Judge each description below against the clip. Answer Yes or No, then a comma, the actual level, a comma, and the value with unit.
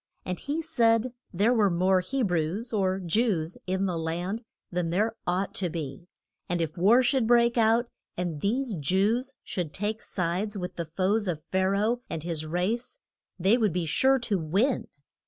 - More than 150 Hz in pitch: Yes, high, 190 Hz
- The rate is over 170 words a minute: Yes, average, 180 wpm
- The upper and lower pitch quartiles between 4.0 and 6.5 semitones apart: Yes, average, 4.7 semitones